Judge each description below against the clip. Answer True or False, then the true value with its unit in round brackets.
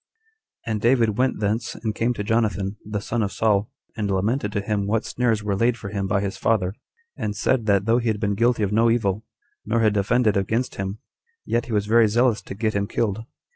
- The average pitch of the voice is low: True (110 Hz)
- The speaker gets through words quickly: True (225 wpm)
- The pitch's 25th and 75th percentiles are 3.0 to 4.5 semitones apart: False (2.4 semitones)